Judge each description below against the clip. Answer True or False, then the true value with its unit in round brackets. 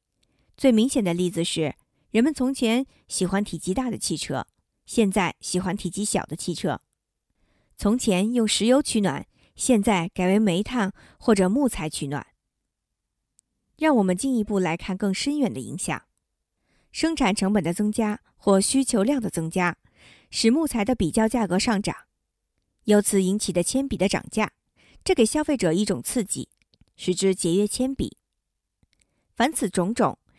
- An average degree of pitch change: True (4.8 semitones)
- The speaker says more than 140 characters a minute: True (225 characters per minute)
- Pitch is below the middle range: False (205 Hz)